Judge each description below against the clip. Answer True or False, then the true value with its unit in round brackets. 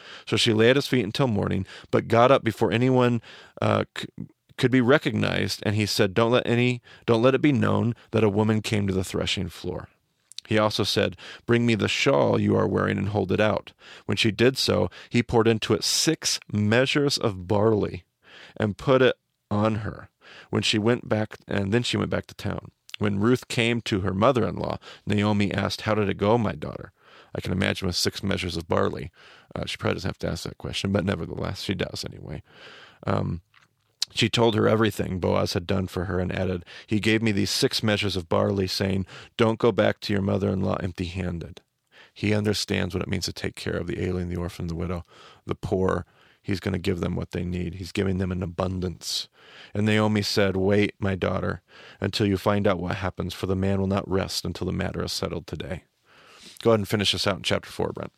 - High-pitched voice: False (105 Hz)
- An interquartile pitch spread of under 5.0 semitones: True (2.9 semitones)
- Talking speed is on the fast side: True (220 wpm)